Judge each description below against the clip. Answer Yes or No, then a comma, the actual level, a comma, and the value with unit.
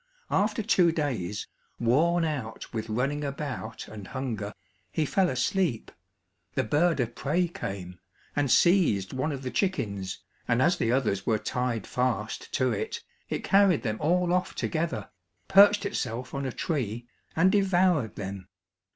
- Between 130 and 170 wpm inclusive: Yes, average, 150 wpm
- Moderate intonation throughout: No, wide, 7.6 semitones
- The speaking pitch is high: No, low, 135 Hz